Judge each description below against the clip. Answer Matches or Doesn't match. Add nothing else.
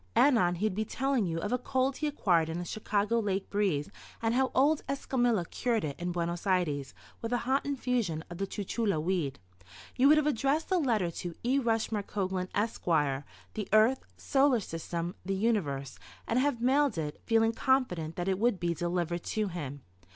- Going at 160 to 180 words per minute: Doesn't match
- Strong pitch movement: Matches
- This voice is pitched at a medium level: Doesn't match